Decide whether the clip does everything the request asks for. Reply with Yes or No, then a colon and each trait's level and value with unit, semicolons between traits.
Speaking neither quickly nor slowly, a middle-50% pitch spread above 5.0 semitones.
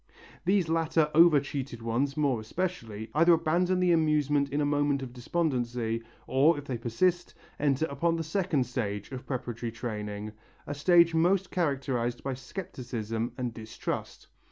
Yes: average, 150 wpm; wide, 5.5 semitones